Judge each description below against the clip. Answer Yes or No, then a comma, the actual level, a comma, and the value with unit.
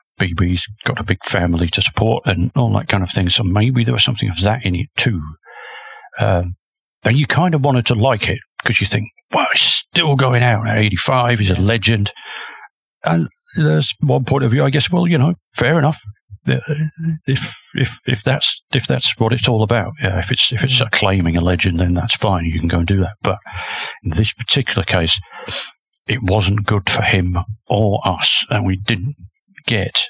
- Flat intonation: No, average, 5.0 semitones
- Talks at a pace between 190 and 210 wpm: Yes, fast, 205 wpm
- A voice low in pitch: Yes, low, 105 Hz